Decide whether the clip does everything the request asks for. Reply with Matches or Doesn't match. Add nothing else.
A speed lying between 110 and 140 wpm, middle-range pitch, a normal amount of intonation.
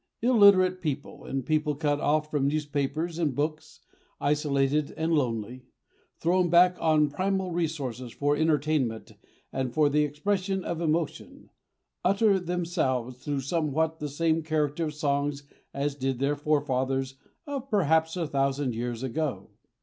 Matches